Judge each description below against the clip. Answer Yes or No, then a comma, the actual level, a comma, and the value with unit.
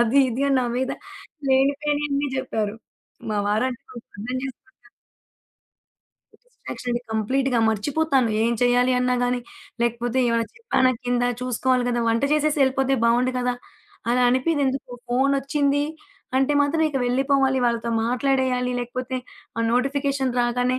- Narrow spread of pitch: Yes, narrow, 2.1 semitones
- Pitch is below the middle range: No, very high, 255 Hz